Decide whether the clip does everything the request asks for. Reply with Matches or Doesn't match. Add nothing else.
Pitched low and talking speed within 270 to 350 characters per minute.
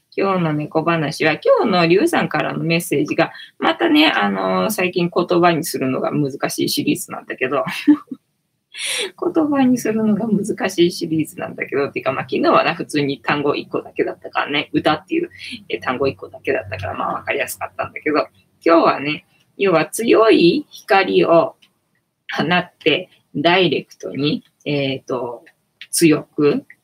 Doesn't match